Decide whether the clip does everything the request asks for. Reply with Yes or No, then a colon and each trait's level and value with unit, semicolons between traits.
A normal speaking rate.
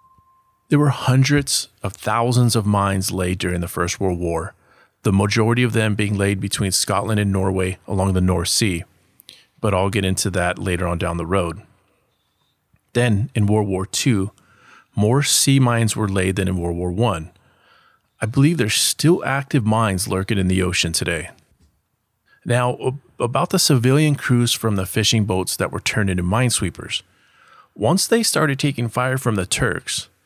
Yes: average, 170 wpm